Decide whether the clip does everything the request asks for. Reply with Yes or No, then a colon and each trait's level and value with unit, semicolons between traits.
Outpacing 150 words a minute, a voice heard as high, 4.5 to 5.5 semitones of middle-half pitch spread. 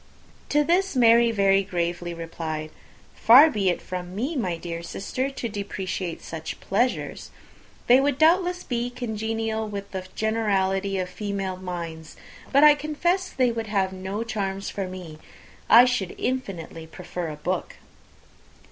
No: average, 145 wpm; high, 200 Hz; average, 5.2 semitones